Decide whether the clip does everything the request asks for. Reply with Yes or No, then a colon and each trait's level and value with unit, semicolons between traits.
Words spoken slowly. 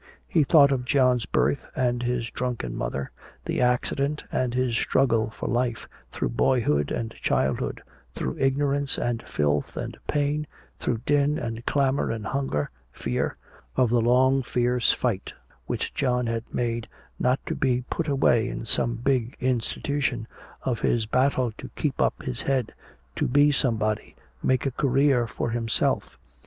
No: average, 150 wpm